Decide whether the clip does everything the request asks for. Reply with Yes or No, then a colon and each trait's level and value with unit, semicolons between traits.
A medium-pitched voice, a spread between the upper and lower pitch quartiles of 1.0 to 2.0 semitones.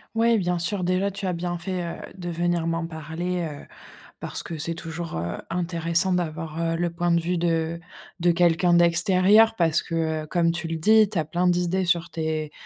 Yes: medium, 170 Hz; narrow, 1.5 semitones